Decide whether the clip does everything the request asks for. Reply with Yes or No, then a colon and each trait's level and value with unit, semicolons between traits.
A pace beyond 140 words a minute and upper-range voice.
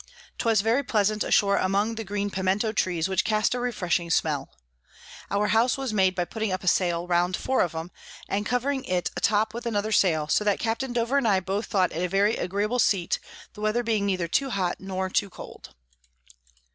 Yes: fast, 205 wpm; high, 200 Hz